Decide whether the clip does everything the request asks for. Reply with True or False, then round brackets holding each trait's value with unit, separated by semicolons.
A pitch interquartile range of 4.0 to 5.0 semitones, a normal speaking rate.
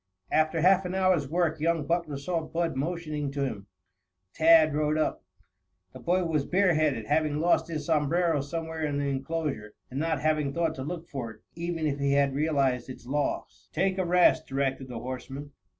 False (3.1 semitones; 185 wpm)